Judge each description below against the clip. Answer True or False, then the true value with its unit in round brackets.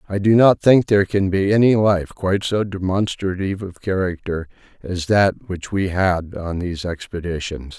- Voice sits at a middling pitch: False (95 Hz)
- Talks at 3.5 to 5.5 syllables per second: True (4.9 syllables/s)